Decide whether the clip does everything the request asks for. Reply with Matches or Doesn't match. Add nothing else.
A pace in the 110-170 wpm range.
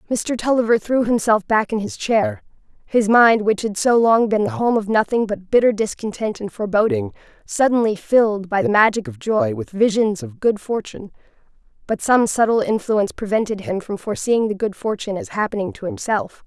Doesn't match